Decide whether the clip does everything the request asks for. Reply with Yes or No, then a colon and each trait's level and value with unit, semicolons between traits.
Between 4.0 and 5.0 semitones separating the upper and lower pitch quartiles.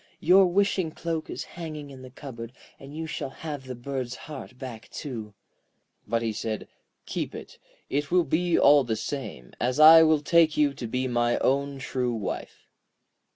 Yes: average, 4.4 semitones